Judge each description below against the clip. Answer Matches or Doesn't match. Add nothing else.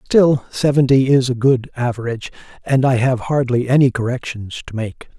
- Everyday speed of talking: Matches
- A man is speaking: Matches